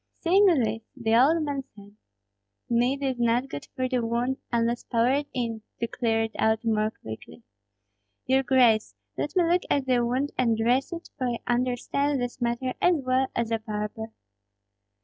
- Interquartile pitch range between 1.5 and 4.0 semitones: Yes, average, 2.8 semitones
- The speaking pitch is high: Yes, high, 245 Hz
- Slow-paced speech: No, average, 170 wpm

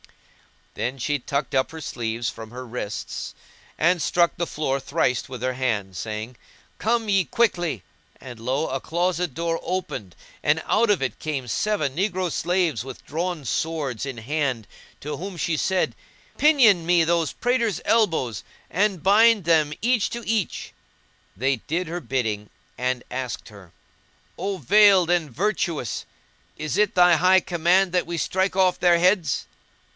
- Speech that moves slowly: No, average, 155 wpm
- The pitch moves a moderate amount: No, wide, 6.3 semitones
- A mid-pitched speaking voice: Yes, medium, 165 Hz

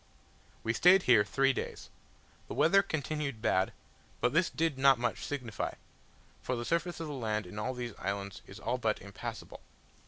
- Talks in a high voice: No, low, 130 Hz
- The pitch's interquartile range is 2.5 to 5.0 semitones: No, wide, 5.6 semitones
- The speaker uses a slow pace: No, average, 175 wpm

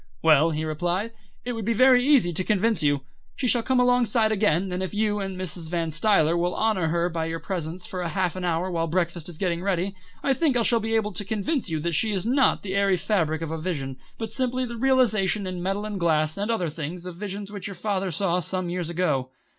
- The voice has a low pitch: No, medium, 185 Hz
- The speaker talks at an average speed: No, fast, 235 wpm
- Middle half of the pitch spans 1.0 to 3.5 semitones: No, average, 4.3 semitones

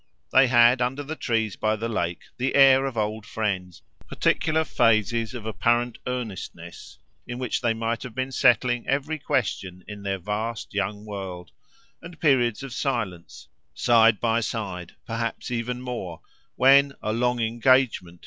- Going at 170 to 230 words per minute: No, average, 150 wpm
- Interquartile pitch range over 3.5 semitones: No, average, 3.2 semitones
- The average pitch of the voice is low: Yes, low, 115 Hz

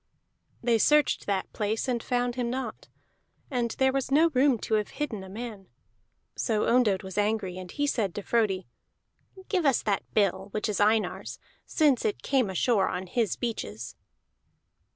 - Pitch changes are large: No, average, 4.1 semitones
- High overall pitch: Yes, high, 220 Hz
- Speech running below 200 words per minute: Yes, average, 165 wpm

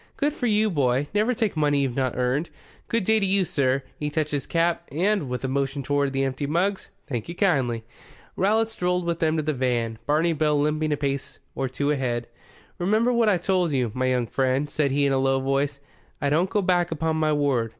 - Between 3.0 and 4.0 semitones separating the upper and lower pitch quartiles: No, average, 4.9 semitones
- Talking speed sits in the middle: No, fast, 225 wpm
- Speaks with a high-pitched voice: No, medium, 150 Hz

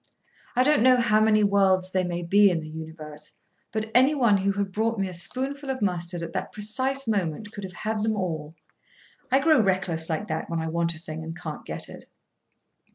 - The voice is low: No, high, 195 Hz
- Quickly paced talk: Yes, fast, 210 wpm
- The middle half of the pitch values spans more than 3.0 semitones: Yes, average, 4.7 semitones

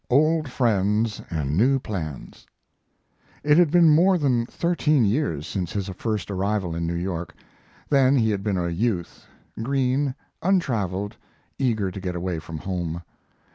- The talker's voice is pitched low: Yes, low, 105 Hz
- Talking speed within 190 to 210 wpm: No, average, 145 wpm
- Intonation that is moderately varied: No, wide, 7.2 semitones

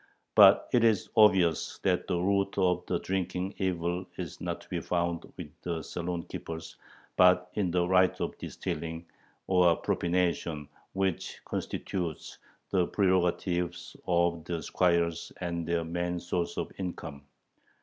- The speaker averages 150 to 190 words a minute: No, average, 140 wpm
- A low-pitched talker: Yes, very low, 90 Hz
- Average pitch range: No, narrow, 1.5 semitones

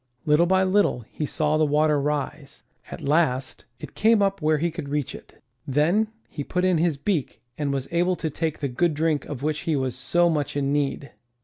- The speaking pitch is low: No, medium, 150 Hz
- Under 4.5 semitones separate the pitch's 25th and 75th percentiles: Yes, average, 3.3 semitones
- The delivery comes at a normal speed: No, fast, 210 wpm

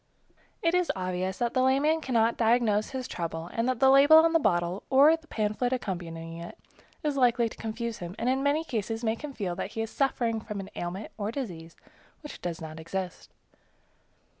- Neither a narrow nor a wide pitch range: No, wide, 6.3 semitones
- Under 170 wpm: No, average, 190 wpm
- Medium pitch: No, high, 225 Hz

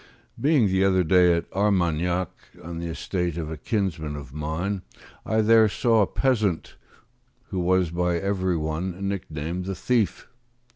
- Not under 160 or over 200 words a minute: No, average, 150 wpm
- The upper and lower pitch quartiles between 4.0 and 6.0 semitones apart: No, average, 2.9 semitones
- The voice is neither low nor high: No, very low, 90 Hz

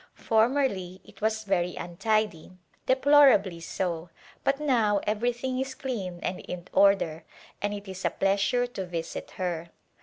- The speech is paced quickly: No, average, 145 wpm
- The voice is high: Yes, high, 205 Hz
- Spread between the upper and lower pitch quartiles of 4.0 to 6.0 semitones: Yes, average, 5.3 semitones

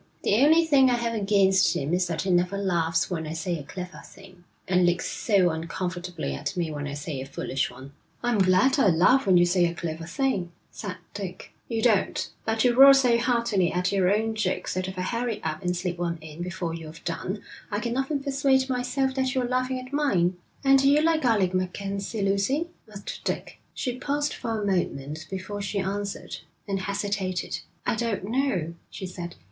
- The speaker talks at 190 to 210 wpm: Yes, average, 200 wpm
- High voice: Yes, high, 195 Hz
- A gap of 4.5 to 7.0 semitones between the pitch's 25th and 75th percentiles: Yes, wide, 5.4 semitones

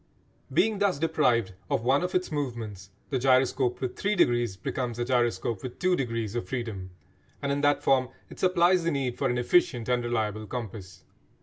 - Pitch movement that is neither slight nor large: Yes, average, 3.8 semitones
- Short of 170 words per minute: No, average, 185 wpm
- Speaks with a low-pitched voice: Yes, low, 125 Hz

